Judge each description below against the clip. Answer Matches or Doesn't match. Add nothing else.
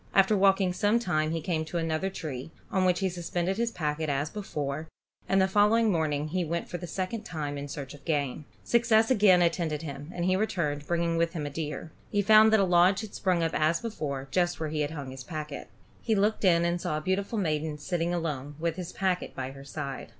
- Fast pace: Matches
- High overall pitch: Doesn't match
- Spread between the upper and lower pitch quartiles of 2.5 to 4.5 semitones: Matches